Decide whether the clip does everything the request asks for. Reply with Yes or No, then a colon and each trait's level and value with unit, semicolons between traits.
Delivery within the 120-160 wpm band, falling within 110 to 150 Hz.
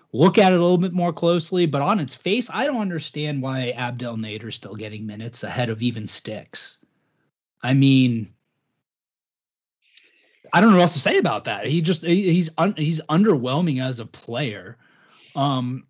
No: average, 175 wpm; medium, 140 Hz